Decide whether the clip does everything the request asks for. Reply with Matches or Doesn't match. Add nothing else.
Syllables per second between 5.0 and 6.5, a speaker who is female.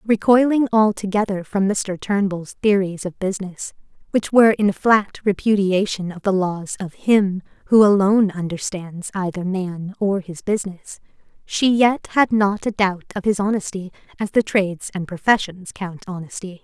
Doesn't match